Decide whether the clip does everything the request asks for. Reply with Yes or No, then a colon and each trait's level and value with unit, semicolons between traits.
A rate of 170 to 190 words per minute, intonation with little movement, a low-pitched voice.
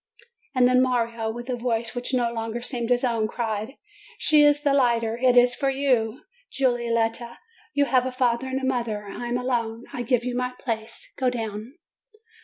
No: average, 185 wpm; narrow, 1.8 semitones; high, 245 Hz